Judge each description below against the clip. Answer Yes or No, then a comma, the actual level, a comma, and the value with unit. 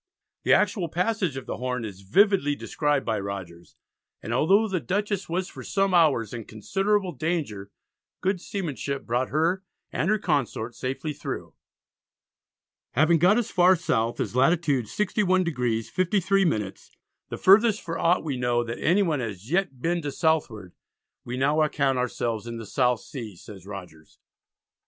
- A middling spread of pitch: No, wide, 7.7 semitones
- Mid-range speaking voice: Yes, medium, 145 Hz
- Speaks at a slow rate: No, average, 150 wpm